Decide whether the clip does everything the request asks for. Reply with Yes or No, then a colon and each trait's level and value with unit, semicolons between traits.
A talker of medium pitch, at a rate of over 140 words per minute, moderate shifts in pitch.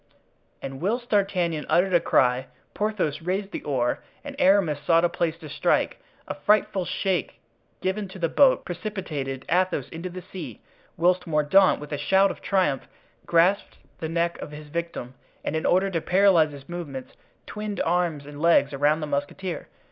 Yes: medium, 170 Hz; average, 170 wpm; average, 4.2 semitones